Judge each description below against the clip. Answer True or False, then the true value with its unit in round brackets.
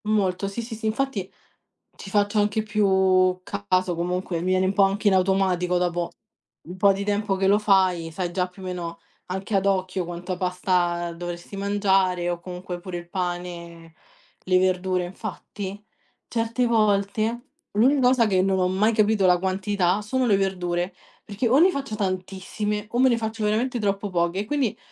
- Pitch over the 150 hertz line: True (190 Hz)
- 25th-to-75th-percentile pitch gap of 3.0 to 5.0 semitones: False (2.6 semitones)